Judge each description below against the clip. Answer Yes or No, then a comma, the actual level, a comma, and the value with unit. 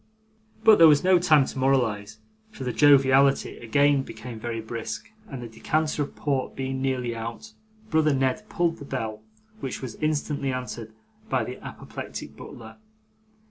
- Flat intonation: No, average, 4.0 semitones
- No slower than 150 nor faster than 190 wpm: Yes, average, 155 wpm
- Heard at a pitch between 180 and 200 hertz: No, low, 130 Hz